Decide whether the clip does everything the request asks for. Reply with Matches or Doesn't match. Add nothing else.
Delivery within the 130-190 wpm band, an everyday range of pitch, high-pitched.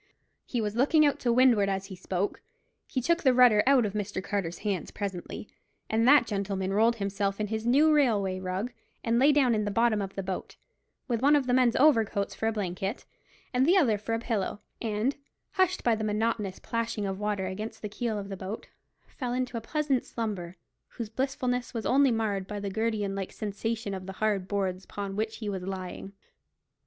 Doesn't match